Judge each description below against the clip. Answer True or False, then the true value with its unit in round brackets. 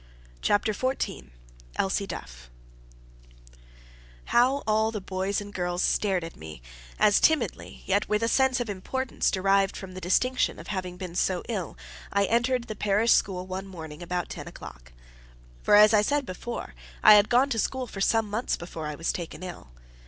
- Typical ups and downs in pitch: True (3.9 semitones)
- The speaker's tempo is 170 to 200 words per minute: True (175 wpm)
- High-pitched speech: True (200 Hz)